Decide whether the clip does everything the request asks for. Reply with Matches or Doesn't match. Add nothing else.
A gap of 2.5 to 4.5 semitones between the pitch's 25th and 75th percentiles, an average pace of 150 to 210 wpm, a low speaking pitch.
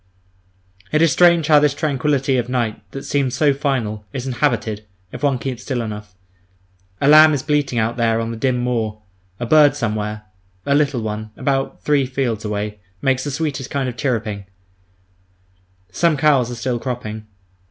Matches